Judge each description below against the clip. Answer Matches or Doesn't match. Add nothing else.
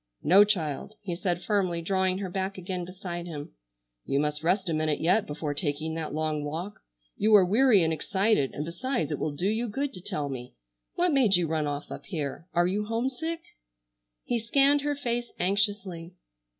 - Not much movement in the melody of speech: Doesn't match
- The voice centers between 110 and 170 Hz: Doesn't match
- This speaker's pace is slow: Doesn't match